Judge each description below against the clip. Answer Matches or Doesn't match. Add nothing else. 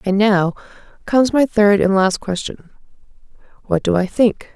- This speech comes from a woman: Matches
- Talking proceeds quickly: Doesn't match